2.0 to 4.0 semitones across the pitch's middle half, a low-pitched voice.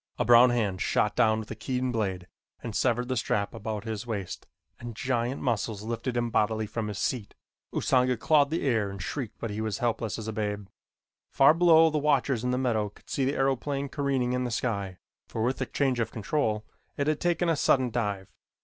Yes: average, 3.4 semitones; low, 120 Hz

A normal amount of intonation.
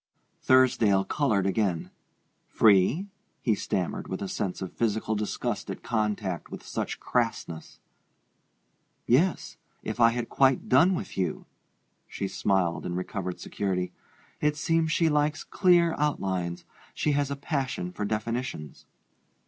No: wide, 6.9 semitones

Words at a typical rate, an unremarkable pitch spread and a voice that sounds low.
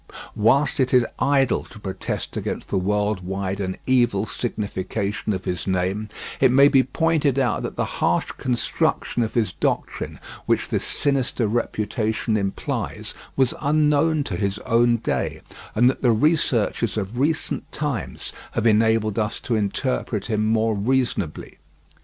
Yes: average, 145 wpm; average, 4.2 semitones; low, 115 Hz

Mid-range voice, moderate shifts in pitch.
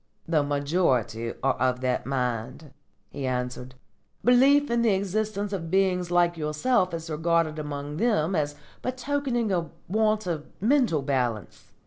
No: medium, 165 Hz; wide, 7.0 semitones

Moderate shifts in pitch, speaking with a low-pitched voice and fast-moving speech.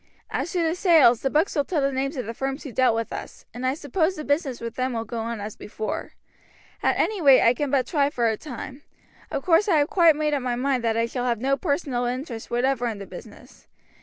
No: average, 3.9 semitones; very high, 265 Hz; fast, 250 wpm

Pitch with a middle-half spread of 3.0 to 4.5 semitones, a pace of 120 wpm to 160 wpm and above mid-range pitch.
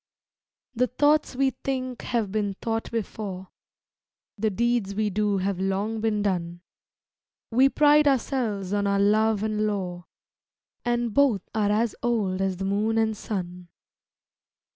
Yes: average, 3.3 semitones; average, 140 wpm; high, 215 Hz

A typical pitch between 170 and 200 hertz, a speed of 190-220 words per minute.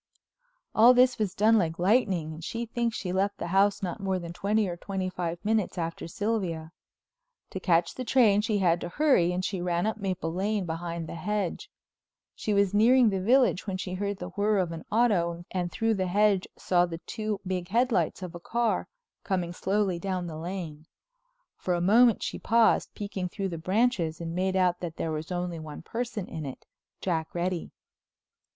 Yes: medium, 185 Hz; average, 195 wpm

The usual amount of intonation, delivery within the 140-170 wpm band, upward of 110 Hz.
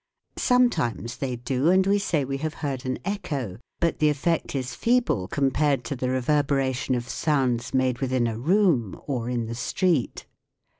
Yes: average, 4.3 semitones; average, 165 wpm; low, 135 Hz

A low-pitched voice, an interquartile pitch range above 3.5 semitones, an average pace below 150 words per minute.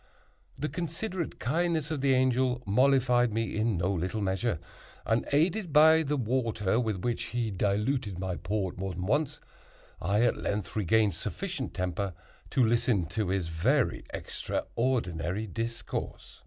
Yes: low, 115 Hz; wide, 5.6 semitones; average, 140 wpm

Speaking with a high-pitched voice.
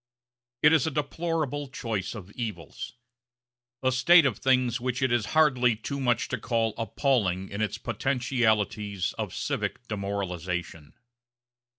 No: low, 120 Hz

